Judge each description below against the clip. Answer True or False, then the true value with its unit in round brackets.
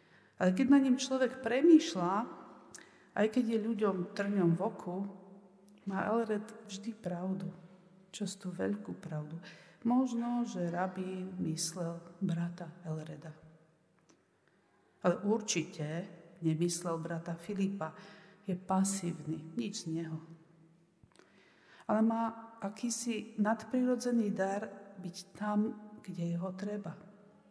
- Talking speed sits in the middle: False (100 wpm)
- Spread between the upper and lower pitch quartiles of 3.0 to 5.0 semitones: True (3.8 semitones)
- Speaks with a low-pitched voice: False (190 Hz)